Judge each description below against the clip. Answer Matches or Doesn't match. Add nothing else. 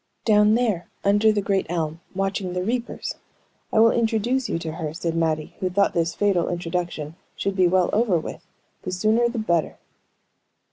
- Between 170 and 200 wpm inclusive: Matches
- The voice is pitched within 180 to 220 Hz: Matches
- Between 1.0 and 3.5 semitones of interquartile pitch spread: Doesn't match